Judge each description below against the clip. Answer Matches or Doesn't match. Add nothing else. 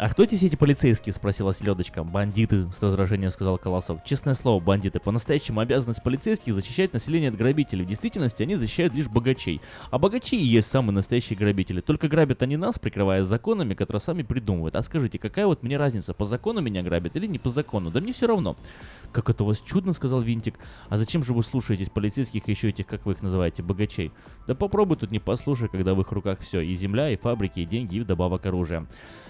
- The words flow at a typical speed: Doesn't match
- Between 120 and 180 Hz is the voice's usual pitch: Doesn't match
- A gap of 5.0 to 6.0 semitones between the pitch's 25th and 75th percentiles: Matches